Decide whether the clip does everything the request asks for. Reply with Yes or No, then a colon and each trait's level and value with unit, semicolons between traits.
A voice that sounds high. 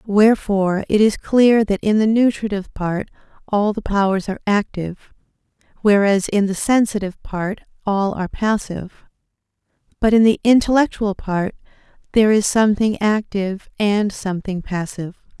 Yes: high, 205 Hz